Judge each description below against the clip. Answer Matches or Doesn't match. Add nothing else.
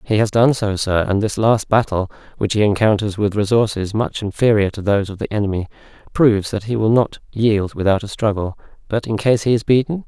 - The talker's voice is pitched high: Doesn't match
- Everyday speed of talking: Doesn't match